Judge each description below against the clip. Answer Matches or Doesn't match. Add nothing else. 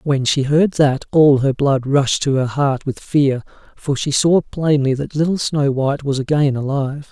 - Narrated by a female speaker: Doesn't match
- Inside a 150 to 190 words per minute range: Doesn't match